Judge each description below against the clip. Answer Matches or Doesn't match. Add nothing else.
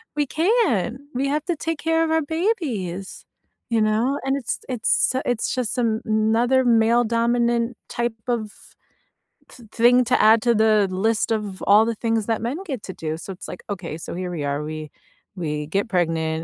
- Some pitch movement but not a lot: Matches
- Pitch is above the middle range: Matches